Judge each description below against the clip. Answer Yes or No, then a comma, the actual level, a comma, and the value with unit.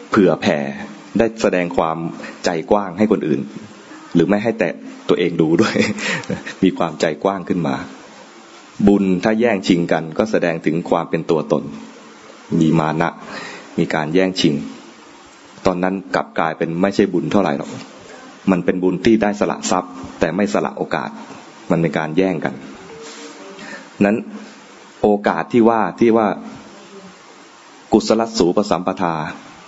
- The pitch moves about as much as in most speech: Yes, average, 3.7 semitones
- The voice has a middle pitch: No, very low, 95 Hz